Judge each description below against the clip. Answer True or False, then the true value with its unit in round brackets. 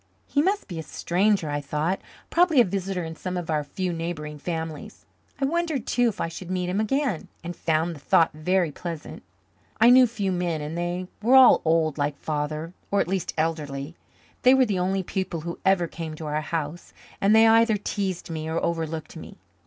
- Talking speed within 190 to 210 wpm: True (200 wpm)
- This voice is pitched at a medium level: True (175 Hz)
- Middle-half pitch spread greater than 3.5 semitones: True (4.0 semitones)